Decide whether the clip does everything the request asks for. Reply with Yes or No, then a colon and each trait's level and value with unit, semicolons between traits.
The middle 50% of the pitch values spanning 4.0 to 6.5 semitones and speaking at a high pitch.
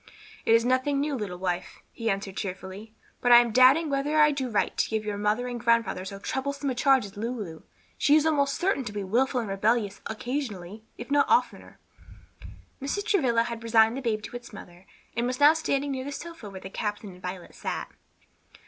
Yes: average, 5.1 semitones; high, 235 Hz